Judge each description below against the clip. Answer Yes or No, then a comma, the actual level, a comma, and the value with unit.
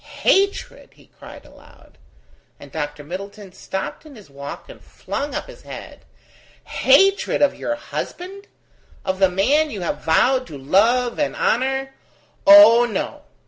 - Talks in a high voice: Yes, high, 240 Hz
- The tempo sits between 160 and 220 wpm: No, average, 140 wpm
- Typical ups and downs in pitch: No, wide, 7.7 semitones